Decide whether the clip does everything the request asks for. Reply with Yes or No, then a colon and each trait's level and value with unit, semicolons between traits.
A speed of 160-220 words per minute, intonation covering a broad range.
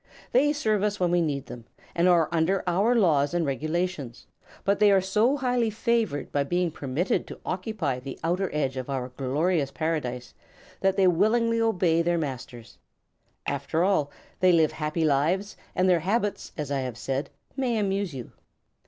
Yes: average, 170 wpm; wide, 5.8 semitones